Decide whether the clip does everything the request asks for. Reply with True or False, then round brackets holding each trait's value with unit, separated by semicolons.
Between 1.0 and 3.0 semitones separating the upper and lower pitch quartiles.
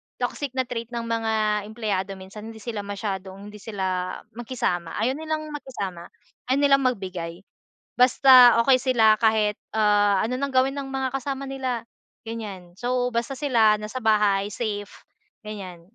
False (4.1 semitones)